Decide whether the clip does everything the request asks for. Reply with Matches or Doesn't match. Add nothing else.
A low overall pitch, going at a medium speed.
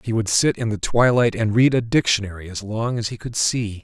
Doesn't match